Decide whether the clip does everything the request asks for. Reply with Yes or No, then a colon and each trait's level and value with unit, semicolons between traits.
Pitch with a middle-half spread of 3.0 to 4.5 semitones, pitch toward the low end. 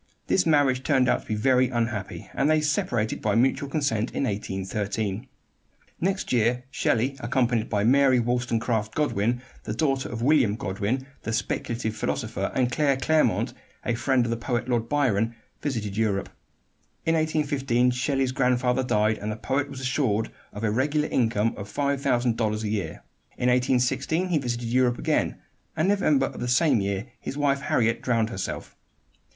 Yes: average, 3.6 semitones; low, 125 Hz